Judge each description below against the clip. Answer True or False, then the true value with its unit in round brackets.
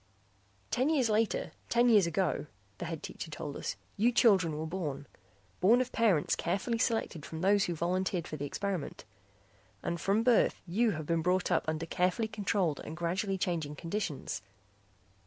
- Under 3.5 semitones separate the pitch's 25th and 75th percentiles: False (4.8 semitones)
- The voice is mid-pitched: True (180 Hz)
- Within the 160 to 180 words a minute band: True (165 wpm)